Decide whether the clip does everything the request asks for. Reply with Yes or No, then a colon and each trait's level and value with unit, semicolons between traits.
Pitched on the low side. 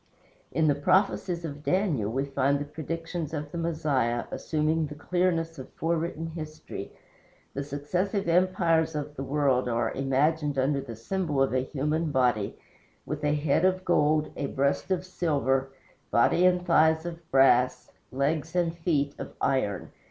No: medium, 150 Hz